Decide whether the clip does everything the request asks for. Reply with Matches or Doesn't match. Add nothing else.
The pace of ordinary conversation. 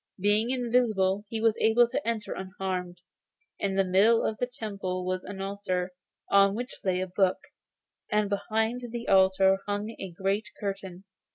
Matches